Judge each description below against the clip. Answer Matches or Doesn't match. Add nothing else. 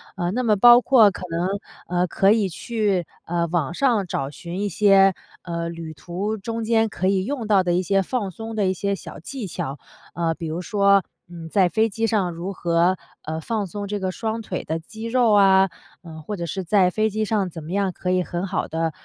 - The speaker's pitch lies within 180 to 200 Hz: Matches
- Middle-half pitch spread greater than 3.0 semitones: Matches